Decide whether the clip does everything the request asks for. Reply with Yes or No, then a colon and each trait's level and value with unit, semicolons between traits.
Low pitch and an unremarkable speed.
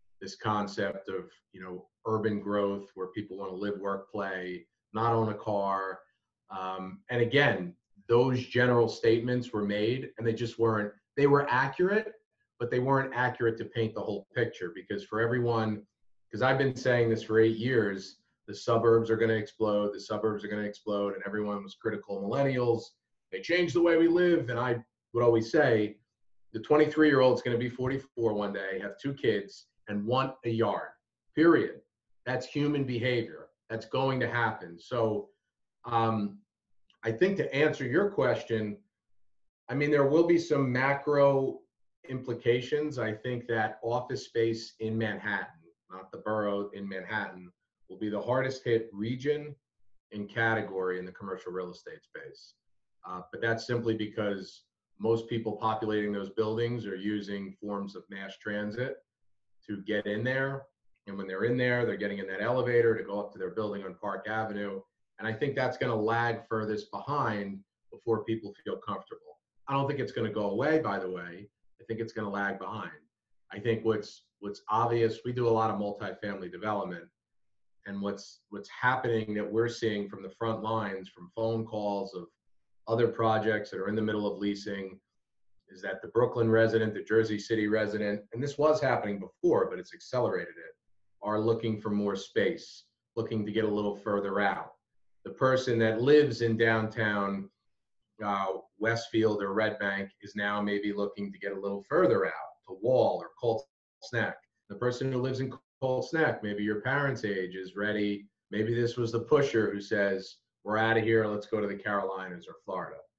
Yes: low, 110 Hz; average, 180 wpm